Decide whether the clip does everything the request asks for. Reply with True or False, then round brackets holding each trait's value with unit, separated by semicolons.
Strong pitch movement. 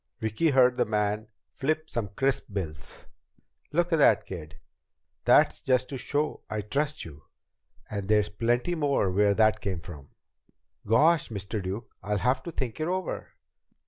True (5.7 semitones)